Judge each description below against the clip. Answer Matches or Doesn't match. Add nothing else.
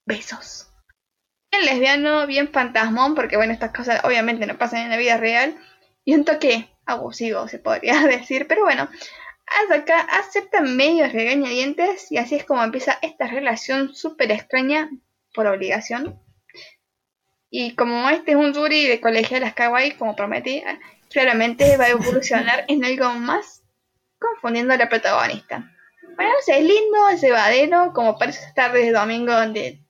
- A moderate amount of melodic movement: Matches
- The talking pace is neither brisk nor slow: Matches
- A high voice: Matches